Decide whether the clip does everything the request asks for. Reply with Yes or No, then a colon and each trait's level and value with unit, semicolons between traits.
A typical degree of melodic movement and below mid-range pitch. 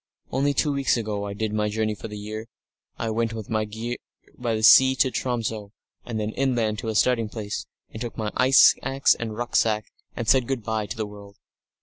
No: narrow, 2.3 semitones; low, 110 Hz